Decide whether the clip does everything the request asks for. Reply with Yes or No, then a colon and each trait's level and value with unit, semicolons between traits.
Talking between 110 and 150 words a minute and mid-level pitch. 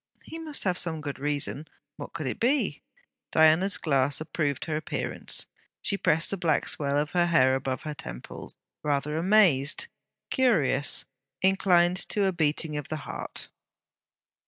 Yes: average, 145 wpm; medium, 155 Hz